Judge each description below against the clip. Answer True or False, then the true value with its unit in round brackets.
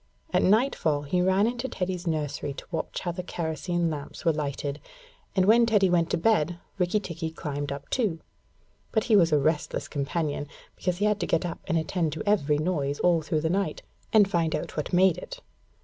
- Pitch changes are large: False (3.9 semitones)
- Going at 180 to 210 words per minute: True (200 wpm)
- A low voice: False (170 Hz)